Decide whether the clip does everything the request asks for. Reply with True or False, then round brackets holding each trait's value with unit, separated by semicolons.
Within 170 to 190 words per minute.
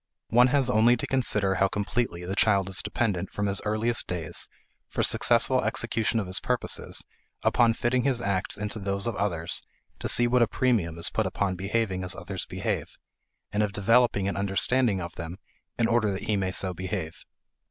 True (185 wpm)